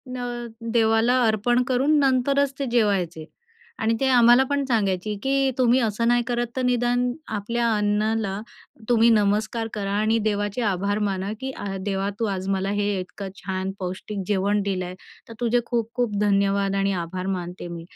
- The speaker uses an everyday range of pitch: Yes, average, 3.5 semitones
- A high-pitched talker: Yes, high, 215 Hz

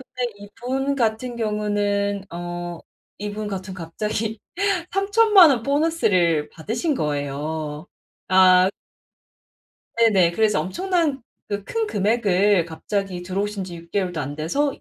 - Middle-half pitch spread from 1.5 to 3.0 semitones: No, average, 5.3 semitones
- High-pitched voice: Yes, high, 205 Hz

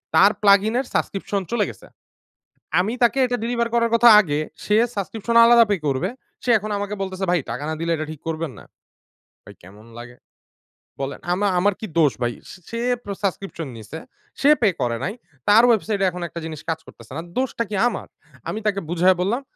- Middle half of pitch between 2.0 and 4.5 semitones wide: No, wide, 5.6 semitones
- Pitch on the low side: No, high, 195 Hz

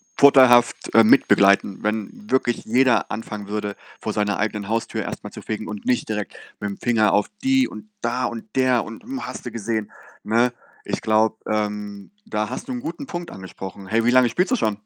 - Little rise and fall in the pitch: No, average, 3.2 semitones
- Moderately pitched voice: No, low, 110 Hz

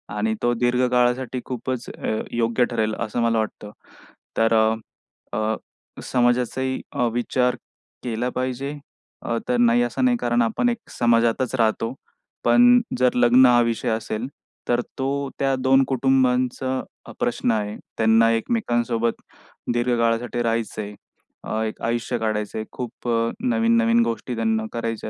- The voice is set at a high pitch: No, low, 120 Hz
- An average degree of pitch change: No, narrow, 2.0 semitones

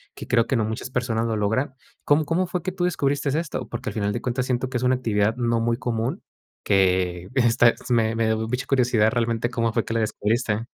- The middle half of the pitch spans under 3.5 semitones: Yes, narrow, 2.5 semitones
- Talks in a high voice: No, low, 120 Hz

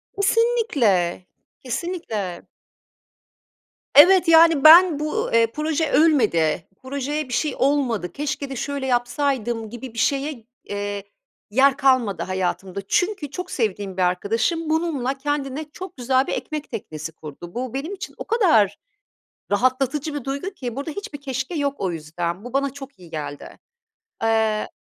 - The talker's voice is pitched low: No, very high, 265 Hz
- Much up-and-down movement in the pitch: Yes, wide, 6.3 semitones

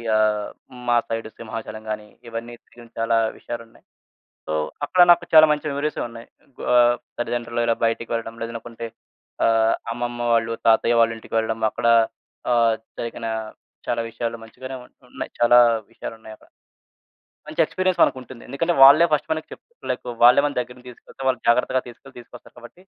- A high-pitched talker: No, low, 120 Hz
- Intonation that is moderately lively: No, narrow, 2.2 semitones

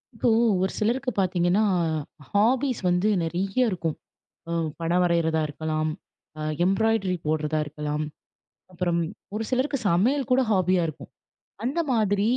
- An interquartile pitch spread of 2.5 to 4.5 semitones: No, average, 5.2 semitones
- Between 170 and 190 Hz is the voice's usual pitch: Yes, medium, 185 Hz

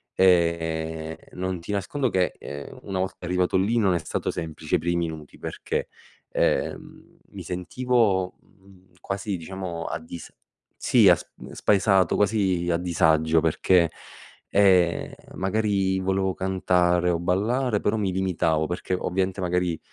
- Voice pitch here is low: Yes, very low, 90 Hz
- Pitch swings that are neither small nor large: No, narrow, 2.3 semitones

